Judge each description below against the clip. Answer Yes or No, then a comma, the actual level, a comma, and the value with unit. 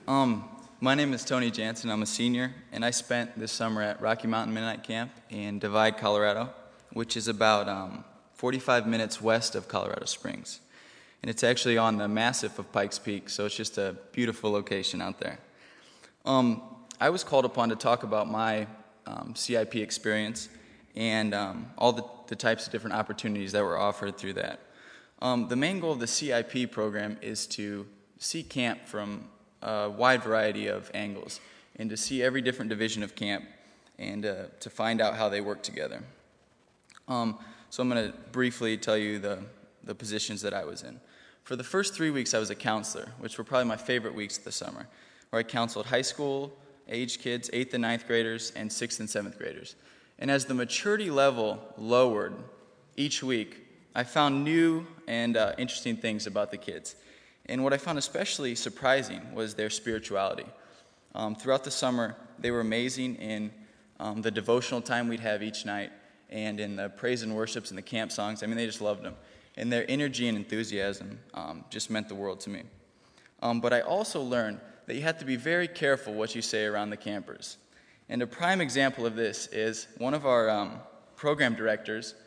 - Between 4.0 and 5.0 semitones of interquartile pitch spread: No, average, 2.7 semitones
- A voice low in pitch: Yes, low, 115 Hz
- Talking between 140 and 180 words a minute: No, average, 190 wpm